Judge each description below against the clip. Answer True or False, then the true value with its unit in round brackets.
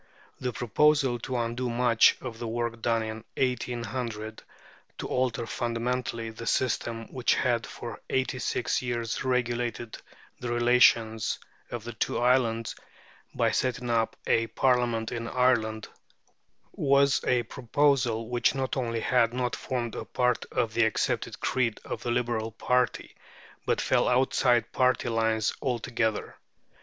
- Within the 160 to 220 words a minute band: False (135 wpm)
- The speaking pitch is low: True (120 Hz)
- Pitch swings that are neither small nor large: False (1.6 semitones)